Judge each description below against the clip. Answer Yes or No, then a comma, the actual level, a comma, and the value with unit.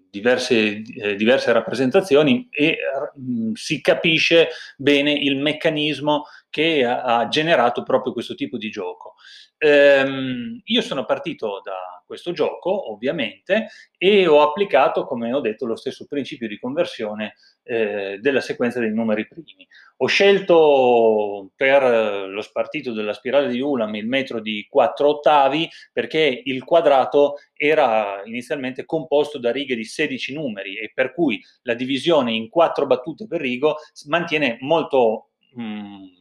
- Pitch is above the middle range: No, medium, 140 Hz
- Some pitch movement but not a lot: No, wide, 5.8 semitones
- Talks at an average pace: Yes, average, 140 wpm